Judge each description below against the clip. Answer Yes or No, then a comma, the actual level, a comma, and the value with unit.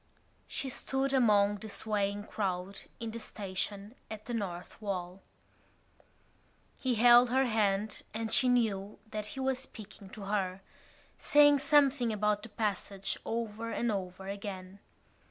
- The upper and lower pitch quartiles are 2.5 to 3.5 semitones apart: Yes, average, 3.2 semitones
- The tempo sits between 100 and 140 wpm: Yes, slow, 135 wpm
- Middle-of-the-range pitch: No, high, 210 Hz